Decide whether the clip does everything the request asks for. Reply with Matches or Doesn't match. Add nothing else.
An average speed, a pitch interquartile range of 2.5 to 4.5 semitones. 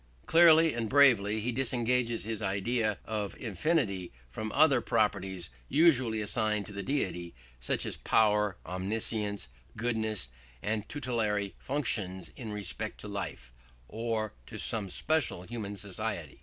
Doesn't match